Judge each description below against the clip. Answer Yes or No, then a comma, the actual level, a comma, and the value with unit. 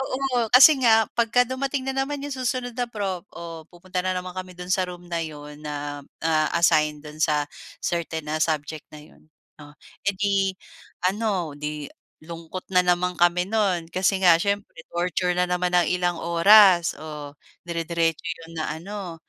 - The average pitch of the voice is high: No, medium, 180 Hz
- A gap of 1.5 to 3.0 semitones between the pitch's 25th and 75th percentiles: No, average, 3.9 semitones